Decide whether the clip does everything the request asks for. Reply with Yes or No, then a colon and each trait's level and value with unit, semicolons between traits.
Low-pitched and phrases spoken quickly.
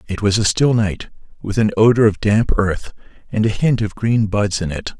Yes: low, 105 Hz; fast, 230 wpm